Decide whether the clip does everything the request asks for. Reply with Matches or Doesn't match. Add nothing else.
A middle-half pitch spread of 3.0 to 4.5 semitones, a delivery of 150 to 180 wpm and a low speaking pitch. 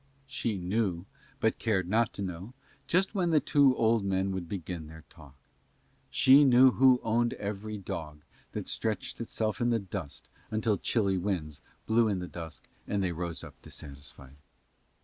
Doesn't match